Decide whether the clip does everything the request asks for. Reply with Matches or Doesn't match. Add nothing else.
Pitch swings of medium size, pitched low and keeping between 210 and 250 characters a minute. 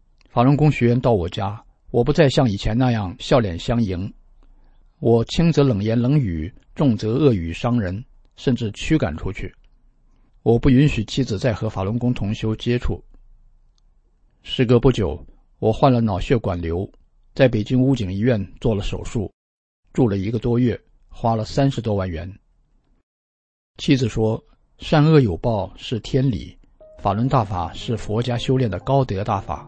Matches